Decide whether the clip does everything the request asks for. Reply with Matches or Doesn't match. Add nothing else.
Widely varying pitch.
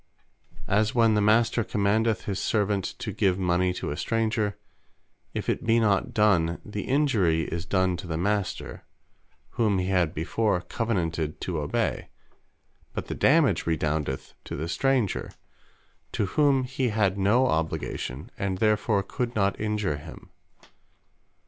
Doesn't match